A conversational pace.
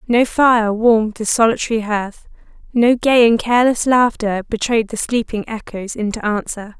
Yes: average, 150 wpm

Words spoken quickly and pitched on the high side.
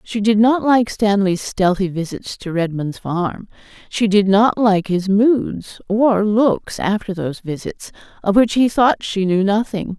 No: average, 170 wpm; high, 205 Hz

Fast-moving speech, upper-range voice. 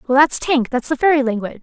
Yes: fast, 260 wpm; very high, 270 Hz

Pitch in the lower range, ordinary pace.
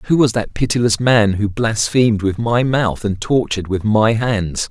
Yes: low, 110 Hz; average, 190 wpm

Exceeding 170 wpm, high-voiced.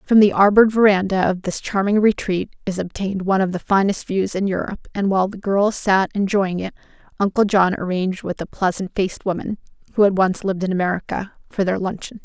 Yes: average, 200 wpm; high, 195 Hz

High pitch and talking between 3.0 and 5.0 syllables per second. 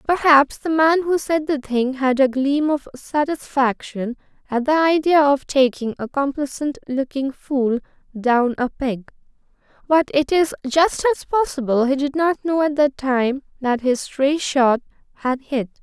Yes: very high, 280 Hz; 4.1 syllables/s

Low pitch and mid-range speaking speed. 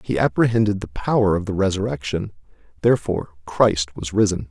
Yes: very low, 95 Hz; average, 145 wpm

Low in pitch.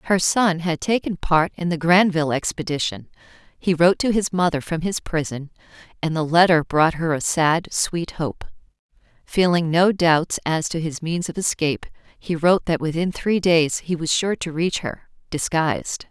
No: medium, 165 Hz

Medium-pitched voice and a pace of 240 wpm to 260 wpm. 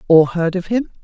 No: medium, 180 Hz; fast, 230 wpm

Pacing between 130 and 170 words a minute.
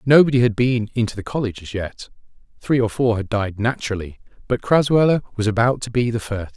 No: average, 200 wpm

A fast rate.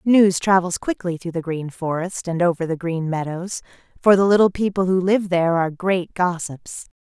No: average, 190 wpm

